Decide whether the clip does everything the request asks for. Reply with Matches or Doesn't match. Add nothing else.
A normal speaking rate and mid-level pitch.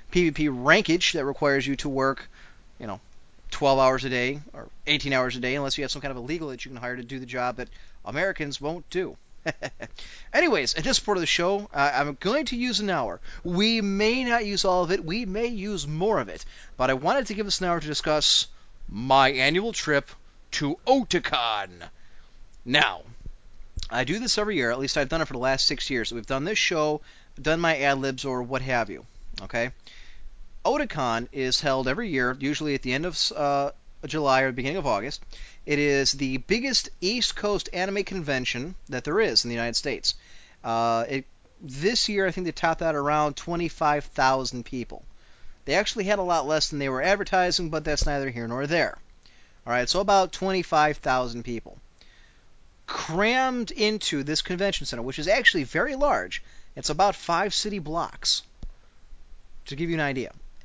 Matches